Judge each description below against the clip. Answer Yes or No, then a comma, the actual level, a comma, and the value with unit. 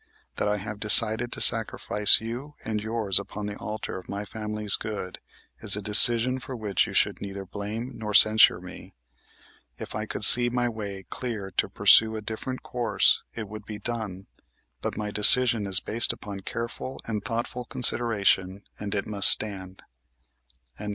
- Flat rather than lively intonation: Yes, narrow, 2.2 semitones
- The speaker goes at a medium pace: Yes, average, 165 wpm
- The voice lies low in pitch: Yes, low, 110 Hz